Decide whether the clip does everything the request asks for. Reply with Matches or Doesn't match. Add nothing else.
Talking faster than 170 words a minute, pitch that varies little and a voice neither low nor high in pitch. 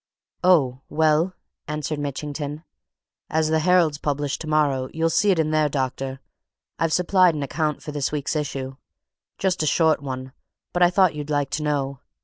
Doesn't match